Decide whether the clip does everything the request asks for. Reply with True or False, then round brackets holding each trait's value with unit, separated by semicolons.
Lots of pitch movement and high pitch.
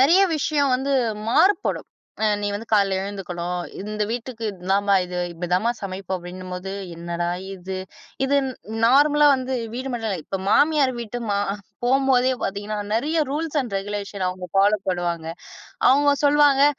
True (6.3 semitones; 210 Hz)